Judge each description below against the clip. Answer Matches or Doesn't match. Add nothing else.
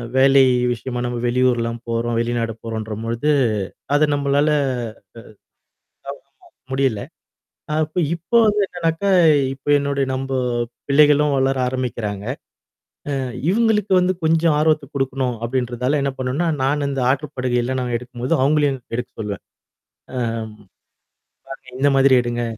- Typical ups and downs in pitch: Matches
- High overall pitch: Doesn't match